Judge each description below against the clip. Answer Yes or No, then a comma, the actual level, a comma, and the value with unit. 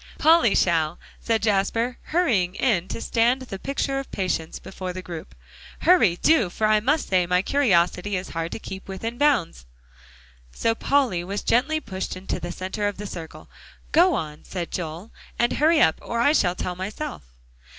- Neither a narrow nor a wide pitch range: No, wide, 6.1 semitones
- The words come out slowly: No, average, 175 wpm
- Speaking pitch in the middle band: No, high, 200 Hz